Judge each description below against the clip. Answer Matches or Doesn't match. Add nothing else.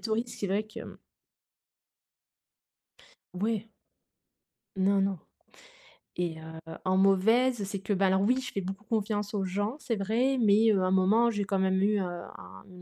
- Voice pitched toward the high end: Matches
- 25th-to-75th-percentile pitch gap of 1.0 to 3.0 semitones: Matches